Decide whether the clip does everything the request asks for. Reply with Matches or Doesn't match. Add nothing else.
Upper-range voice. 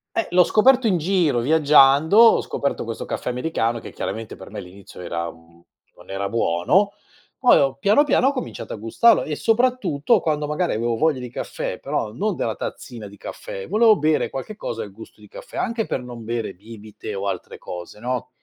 Doesn't match